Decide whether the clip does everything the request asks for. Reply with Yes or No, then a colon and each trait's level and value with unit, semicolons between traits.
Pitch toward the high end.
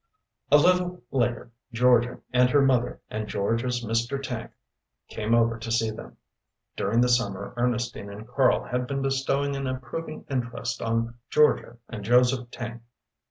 No: low, 120 Hz